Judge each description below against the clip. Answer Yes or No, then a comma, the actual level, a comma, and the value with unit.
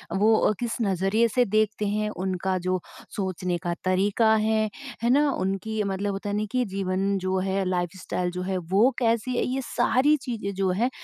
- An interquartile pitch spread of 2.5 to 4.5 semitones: Yes, average, 2.8 semitones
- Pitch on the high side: Yes, high, 200 Hz